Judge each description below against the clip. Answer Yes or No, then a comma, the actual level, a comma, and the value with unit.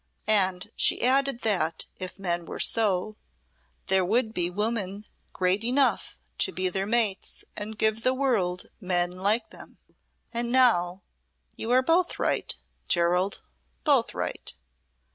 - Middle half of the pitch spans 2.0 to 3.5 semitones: No, average, 4.5 semitones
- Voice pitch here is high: Yes, high, 205 Hz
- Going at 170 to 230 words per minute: No, slow, 135 wpm